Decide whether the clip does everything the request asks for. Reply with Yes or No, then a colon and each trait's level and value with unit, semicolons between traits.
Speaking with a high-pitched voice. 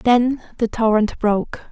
Yes: high, 225 Hz